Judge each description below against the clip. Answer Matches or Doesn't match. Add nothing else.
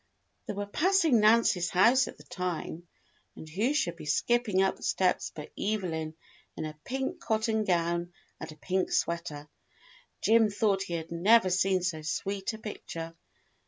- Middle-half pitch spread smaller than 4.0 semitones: Doesn't match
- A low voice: Doesn't match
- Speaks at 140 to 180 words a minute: Matches